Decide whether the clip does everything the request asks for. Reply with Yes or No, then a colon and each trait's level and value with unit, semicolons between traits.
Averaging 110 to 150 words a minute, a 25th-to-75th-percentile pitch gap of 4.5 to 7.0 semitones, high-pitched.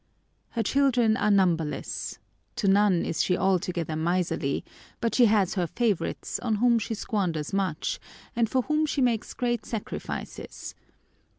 Yes: average, 140 wpm; average, 4.8 semitones; high, 205 Hz